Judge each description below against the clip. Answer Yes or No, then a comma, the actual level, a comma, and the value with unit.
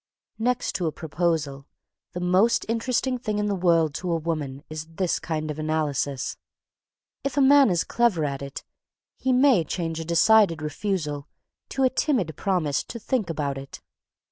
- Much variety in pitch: Yes, wide, 6.2 semitones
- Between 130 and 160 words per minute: No, average, 170 wpm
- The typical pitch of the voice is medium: Yes, medium, 170 Hz